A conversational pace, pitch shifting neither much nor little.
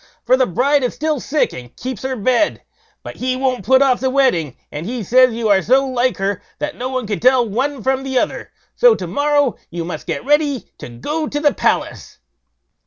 No: fast, 215 wpm; average, 3.4 semitones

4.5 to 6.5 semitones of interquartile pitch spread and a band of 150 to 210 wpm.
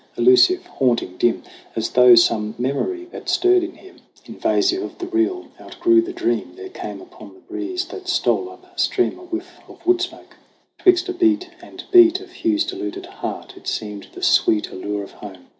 No: average, 3.2 semitones; average, 190 wpm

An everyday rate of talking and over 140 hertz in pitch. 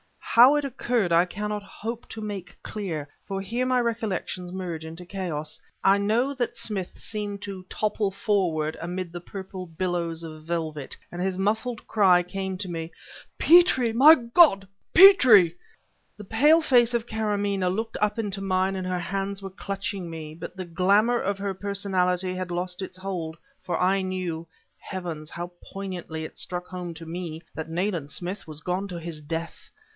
Yes: average, 170 wpm; high, 190 Hz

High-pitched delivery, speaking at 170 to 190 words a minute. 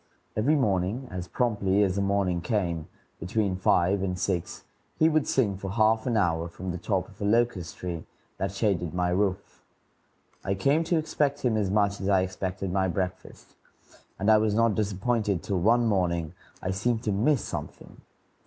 No: low, 100 Hz; average, 180 wpm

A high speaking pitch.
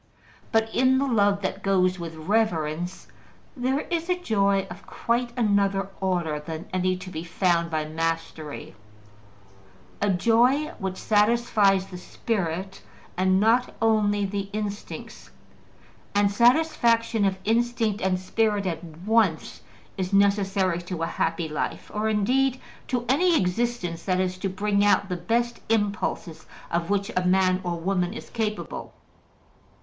Yes: high, 200 Hz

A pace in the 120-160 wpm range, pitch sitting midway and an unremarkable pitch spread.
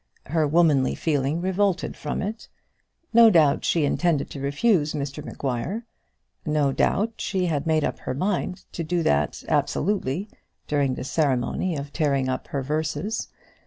Yes: average, 145 wpm; medium, 155 Hz; average, 4.5 semitones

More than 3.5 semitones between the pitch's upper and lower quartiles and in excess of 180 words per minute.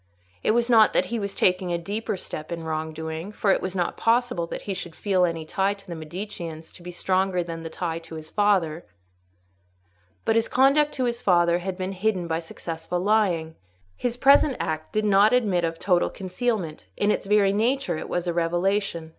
Yes: average, 4.0 semitones; average, 200 wpm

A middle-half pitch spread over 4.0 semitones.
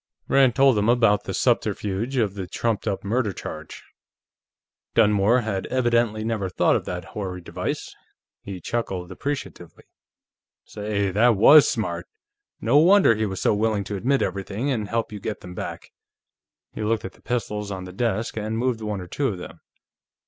No: average, 3.3 semitones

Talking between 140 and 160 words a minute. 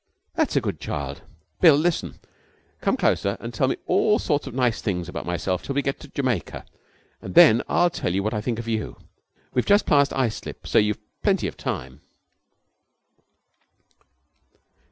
No: average, 170 wpm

